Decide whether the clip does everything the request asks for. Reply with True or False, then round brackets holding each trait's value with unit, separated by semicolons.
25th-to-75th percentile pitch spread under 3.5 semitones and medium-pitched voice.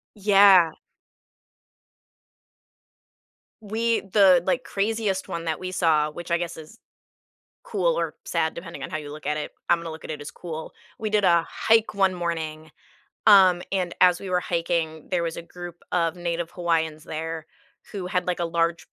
True (2.9 semitones; 175 Hz)